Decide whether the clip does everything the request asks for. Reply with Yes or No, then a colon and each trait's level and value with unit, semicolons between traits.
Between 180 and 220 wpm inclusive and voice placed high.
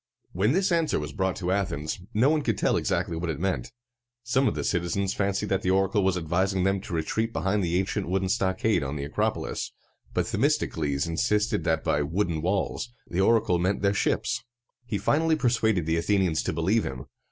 No: average, 195 wpm; very low, 95 Hz